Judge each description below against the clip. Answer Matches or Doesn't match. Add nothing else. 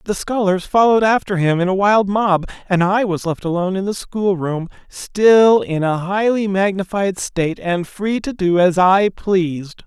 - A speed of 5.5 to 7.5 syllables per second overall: Doesn't match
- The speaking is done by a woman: Doesn't match